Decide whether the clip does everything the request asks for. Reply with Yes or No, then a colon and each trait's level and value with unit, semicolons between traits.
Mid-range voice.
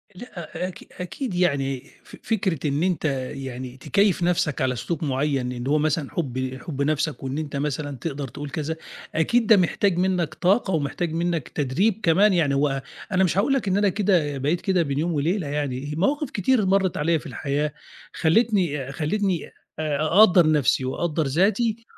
Yes: medium, 160 Hz